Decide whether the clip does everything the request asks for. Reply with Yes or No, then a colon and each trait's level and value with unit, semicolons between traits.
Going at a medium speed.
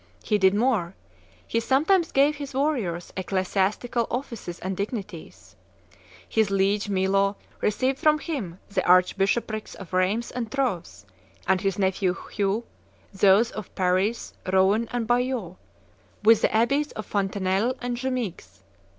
No: slow, 130 wpm